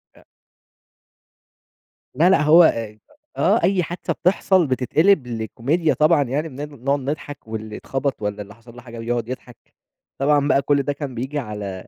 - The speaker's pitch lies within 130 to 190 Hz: Yes, medium, 140 Hz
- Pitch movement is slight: No, average, 4.6 semitones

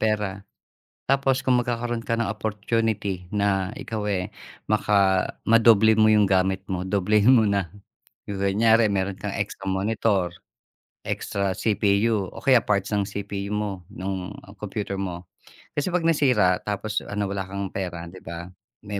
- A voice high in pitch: No, low, 100 Hz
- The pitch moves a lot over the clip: No, narrow, 2.4 semitones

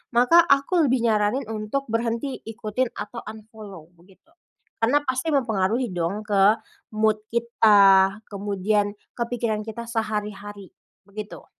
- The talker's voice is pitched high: Yes, high, 215 Hz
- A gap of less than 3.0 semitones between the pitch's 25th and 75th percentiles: Yes, narrow, 2.6 semitones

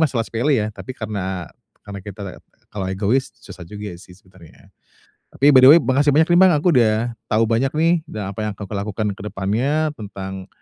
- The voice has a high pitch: No, low, 110 Hz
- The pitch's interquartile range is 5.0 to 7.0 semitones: Yes, wide, 5.5 semitones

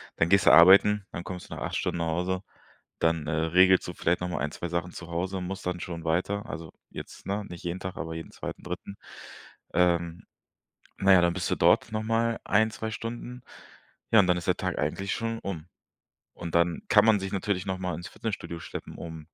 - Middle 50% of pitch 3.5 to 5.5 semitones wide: No, average, 2.7 semitones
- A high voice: No, very low, 90 Hz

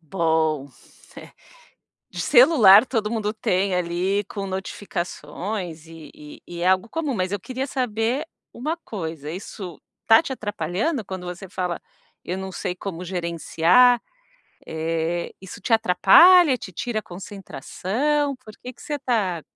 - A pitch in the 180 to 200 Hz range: Yes, high, 190 Hz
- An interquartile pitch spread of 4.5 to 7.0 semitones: Yes, average, 5.3 semitones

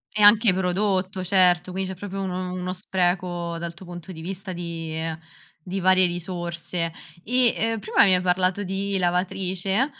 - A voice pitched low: No, medium, 185 Hz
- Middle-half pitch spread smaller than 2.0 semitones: Yes, narrow, 1.6 semitones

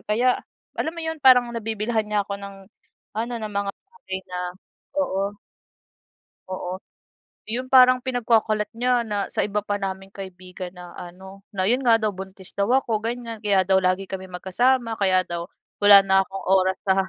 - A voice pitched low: No, high, 205 Hz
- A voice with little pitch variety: No, average, 3.7 semitones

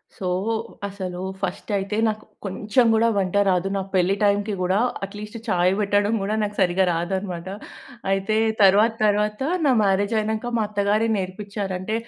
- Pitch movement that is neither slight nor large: No, narrow, 1.9 semitones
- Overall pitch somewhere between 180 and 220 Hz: Yes, high, 200 Hz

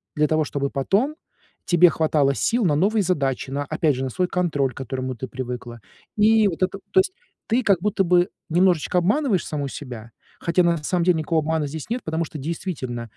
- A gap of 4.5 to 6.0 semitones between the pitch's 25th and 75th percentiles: Yes, average, 5.0 semitones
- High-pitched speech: No, medium, 160 Hz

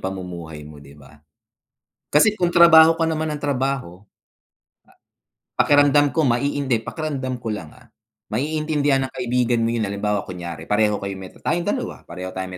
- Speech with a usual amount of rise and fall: No, wide, 7.5 semitones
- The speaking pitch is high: No, low, 120 Hz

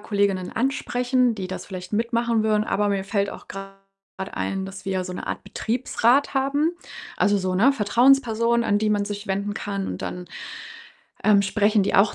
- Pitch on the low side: No, high, 205 Hz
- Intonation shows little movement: No, average, 3.1 semitones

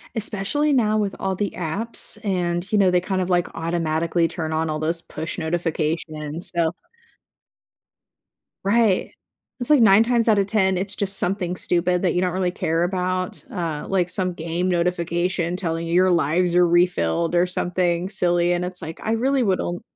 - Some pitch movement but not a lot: No, narrow, 2.3 semitones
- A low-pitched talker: No, medium, 180 Hz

